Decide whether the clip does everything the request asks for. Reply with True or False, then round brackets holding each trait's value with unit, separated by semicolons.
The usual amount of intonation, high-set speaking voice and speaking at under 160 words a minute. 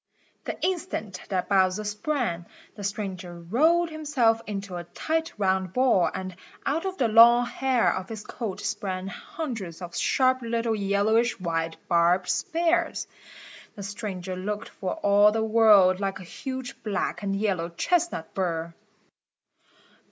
True (4.7 semitones; 205 Hz; 140 wpm)